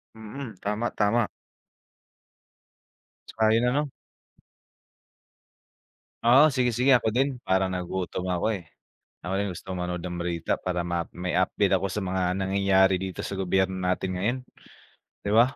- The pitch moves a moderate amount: Yes, average, 3.4 semitones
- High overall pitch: No, very low, 95 Hz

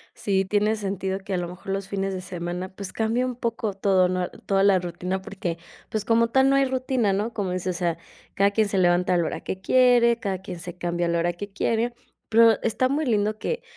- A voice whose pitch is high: Yes, high, 195 Hz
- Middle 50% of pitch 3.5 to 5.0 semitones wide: Yes, average, 3.8 semitones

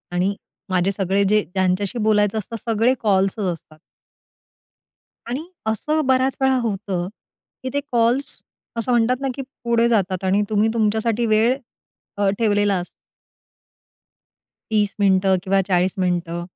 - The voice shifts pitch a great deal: No, average, 3.5 semitones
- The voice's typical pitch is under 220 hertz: Yes, high, 210 Hz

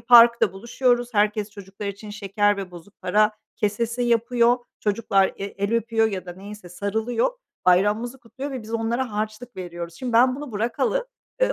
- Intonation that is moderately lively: Yes, average, 3.0 semitones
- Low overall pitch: No, high, 220 Hz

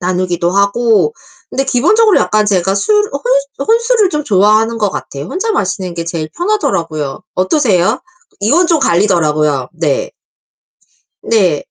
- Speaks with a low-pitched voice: No, high, 215 Hz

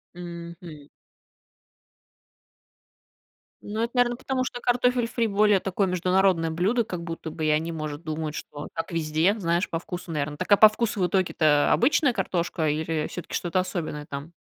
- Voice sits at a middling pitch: Yes, medium, 175 Hz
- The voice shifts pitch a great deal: No, average, 4.5 semitones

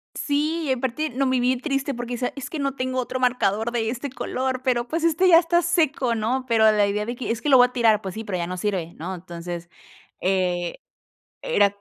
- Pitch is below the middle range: No, high, 245 Hz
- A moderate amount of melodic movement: Yes, average, 4.7 semitones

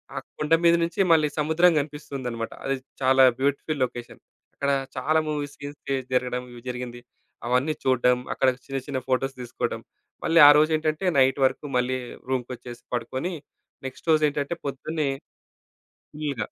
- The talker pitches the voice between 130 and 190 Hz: Yes, low, 135 Hz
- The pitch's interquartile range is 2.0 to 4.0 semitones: Yes, average, 3.1 semitones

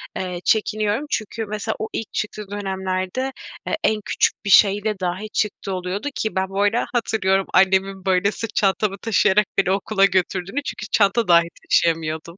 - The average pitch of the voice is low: No, high, 195 Hz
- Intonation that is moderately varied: No, narrow, 2.2 semitones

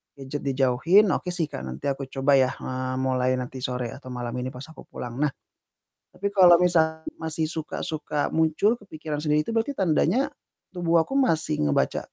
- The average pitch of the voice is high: No, medium, 150 Hz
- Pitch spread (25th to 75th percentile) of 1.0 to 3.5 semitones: No, average, 4.9 semitones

